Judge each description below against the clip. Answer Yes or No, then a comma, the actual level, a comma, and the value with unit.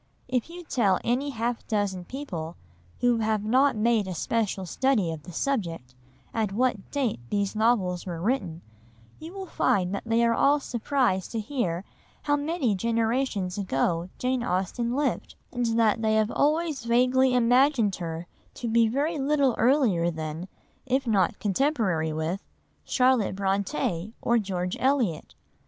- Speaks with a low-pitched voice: No, high, 225 Hz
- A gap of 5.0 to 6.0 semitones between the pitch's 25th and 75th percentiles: Yes, wide, 5.6 semitones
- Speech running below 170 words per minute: Yes, average, 150 wpm